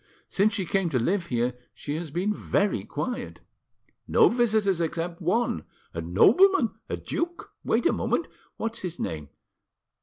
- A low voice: No, medium, 185 Hz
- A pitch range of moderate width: No, wide, 6.2 semitones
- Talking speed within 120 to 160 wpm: Yes, average, 140 wpm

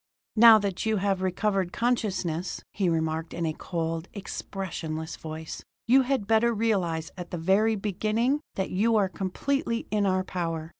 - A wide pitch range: No, average, 4.6 semitones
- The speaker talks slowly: No, average, 155 wpm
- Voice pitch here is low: No, high, 190 Hz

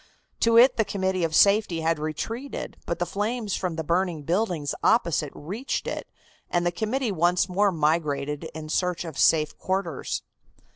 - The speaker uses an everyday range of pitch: Yes, average, 4.3 semitones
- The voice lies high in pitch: No, medium, 175 Hz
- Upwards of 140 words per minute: Yes, average, 160 wpm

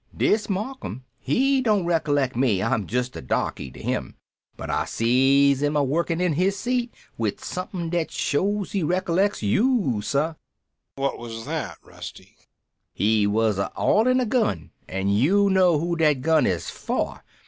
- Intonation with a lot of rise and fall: Yes, wide, 8.5 semitones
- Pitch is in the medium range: Yes, medium, 155 Hz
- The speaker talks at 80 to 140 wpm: No, average, 160 wpm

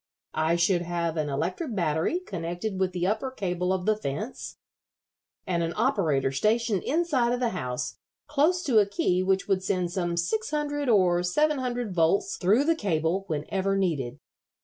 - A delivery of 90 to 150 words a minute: No, average, 170 wpm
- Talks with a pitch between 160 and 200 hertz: Yes, high, 190 Hz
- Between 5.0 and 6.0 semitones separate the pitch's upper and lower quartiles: Yes, wide, 5.5 semitones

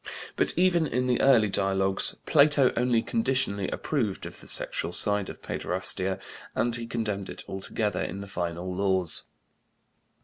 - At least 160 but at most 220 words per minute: No, average, 145 wpm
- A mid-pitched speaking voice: No, low, 105 Hz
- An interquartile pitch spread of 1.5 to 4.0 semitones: No, average, 4.7 semitones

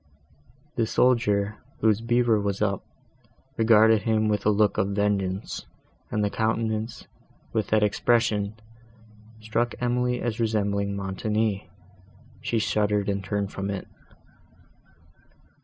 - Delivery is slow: Yes, slow, 115 wpm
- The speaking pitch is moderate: No, low, 105 Hz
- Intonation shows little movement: Yes, narrow, 1.9 semitones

